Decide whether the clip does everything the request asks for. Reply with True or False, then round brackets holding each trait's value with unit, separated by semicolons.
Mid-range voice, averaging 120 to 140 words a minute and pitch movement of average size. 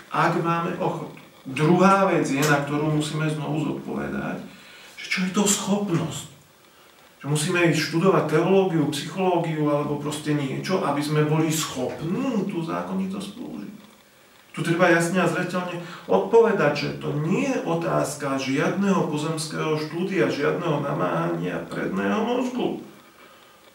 True (165 Hz; 125 wpm; 3.9 semitones)